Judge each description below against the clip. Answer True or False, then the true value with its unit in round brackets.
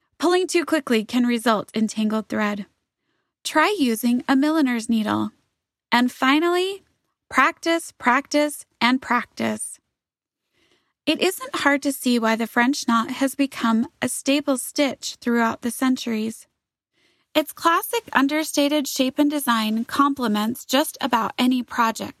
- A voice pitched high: True (255 Hz)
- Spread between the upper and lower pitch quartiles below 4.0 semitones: False (4.4 semitones)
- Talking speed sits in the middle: False (125 wpm)